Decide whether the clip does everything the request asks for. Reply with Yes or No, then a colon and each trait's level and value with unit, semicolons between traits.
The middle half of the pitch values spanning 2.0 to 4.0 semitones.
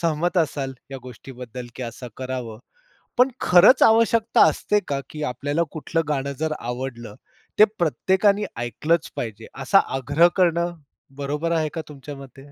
No: average, 4.9 semitones